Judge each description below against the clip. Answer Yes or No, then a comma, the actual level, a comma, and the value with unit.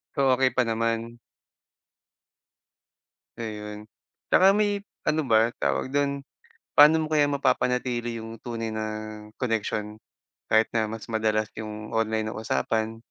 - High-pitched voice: No, low, 115 Hz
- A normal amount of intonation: Yes, average, 3.3 semitones